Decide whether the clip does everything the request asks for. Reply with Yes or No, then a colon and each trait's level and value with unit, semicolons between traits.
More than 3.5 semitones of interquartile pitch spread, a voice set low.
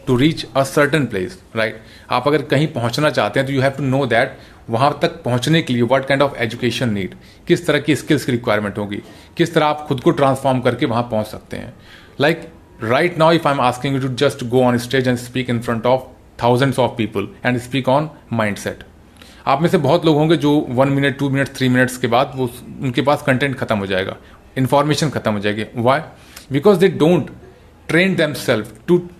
Yes: average, 4.3 semitones; low, 130 Hz